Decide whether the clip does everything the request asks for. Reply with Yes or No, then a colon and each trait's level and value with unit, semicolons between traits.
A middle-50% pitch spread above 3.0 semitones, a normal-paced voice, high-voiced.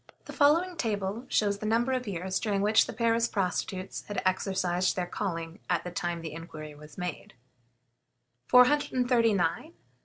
Yes: average, 4.7 semitones; average, 150 wpm; high, 200 Hz